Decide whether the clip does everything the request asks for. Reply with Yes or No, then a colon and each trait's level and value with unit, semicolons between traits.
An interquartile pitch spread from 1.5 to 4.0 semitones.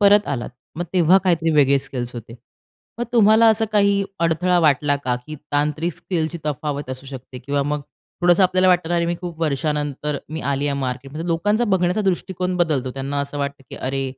No: average, 4.4 semitones